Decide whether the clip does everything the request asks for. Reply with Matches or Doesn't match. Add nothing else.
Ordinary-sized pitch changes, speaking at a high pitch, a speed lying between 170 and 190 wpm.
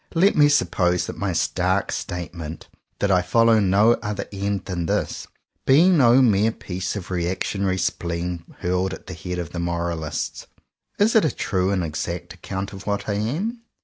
Doesn't match